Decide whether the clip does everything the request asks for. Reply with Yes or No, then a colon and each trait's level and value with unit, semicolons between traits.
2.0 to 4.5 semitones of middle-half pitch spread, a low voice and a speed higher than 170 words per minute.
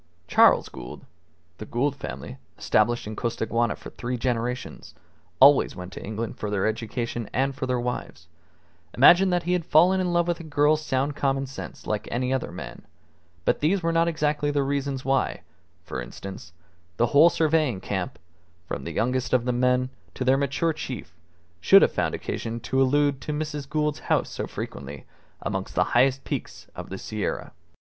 Yes: average, 4.2 semitones; low, 130 Hz; average, 180 wpm